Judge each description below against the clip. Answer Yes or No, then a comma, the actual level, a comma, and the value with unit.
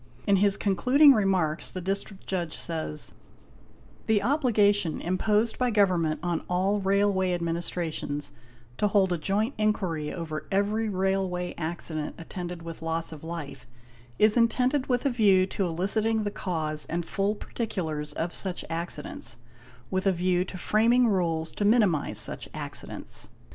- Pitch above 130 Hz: Yes, high, 190 Hz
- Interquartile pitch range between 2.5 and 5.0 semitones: Yes, average, 3.9 semitones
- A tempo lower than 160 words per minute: Yes, average, 145 wpm